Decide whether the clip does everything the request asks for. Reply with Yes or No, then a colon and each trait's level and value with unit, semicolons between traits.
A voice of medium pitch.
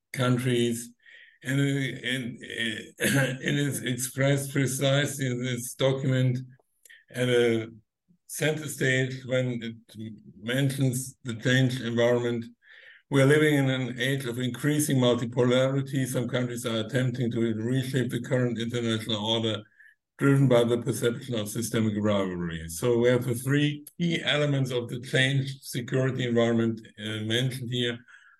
No: low, 125 Hz